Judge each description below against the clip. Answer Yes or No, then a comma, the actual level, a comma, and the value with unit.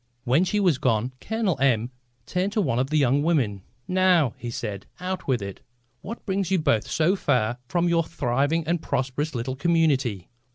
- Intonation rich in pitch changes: Yes, wide, 6.0 semitones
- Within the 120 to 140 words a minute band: No, average, 180 wpm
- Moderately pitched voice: Yes, medium, 145 Hz